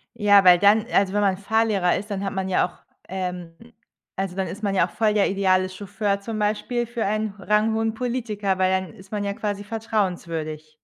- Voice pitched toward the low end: No, high, 200 Hz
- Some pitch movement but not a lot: No, narrow, 2.3 semitones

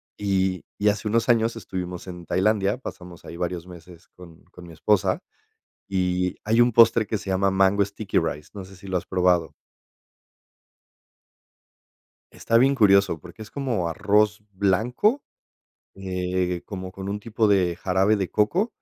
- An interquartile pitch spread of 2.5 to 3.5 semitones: Yes, average, 2.8 semitones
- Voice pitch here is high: No, very low, 95 Hz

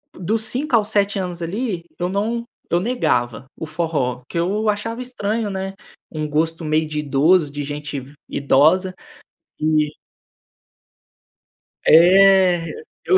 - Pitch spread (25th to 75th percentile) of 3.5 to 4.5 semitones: No, average, 5.1 semitones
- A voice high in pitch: No, medium, 175 Hz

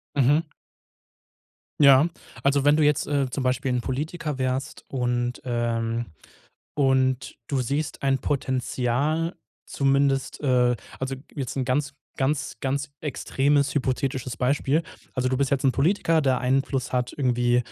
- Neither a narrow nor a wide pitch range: No, narrow, 2.0 semitones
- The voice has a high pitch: No, low, 135 Hz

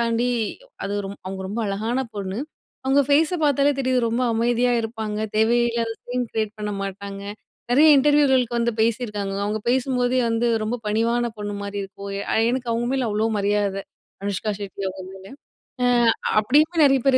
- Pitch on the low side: No, high, 230 Hz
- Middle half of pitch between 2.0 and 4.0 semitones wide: Yes, average, 3.5 semitones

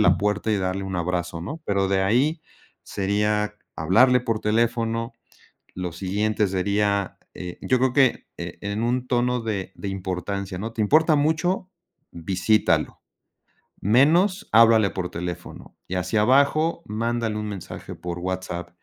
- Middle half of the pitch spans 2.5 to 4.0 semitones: No, average, 4.4 semitones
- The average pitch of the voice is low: Yes, low, 105 Hz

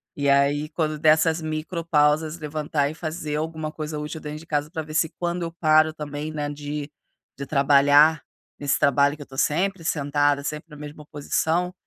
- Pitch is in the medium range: Yes, medium, 150 Hz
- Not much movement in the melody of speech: Yes, narrow, 1.5 semitones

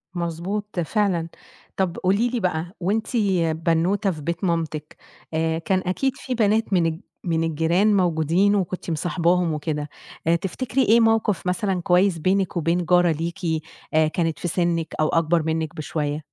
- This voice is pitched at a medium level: Yes, medium, 175 Hz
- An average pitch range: Yes, average, 3.2 semitones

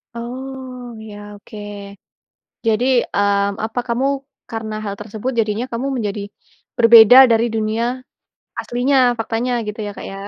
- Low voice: No, high, 225 Hz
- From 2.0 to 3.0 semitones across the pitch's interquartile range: Yes, narrow, 2.6 semitones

